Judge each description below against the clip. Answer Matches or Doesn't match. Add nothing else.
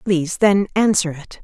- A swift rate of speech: Doesn't match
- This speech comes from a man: Doesn't match